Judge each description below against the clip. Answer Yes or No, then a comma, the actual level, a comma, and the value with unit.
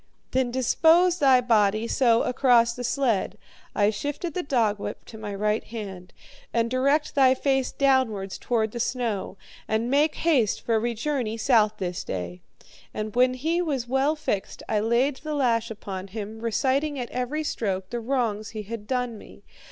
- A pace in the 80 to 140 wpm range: No, average, 165 wpm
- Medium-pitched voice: No, high, 235 Hz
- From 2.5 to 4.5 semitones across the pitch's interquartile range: Yes, average, 3.7 semitones